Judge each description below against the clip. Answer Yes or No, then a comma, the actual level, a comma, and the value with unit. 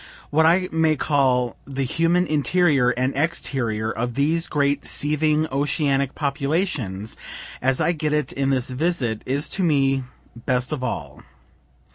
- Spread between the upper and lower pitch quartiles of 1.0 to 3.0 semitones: No, average, 3.5 semitones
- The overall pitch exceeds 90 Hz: Yes, medium, 140 Hz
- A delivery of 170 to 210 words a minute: No, average, 140 wpm